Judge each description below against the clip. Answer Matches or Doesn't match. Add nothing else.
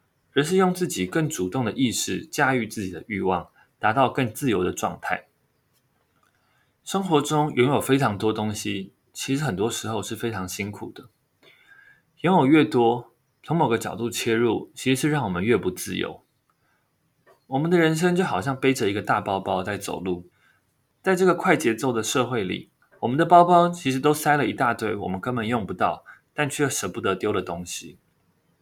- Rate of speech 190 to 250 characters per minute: Doesn't match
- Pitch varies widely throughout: Matches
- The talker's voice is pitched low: Matches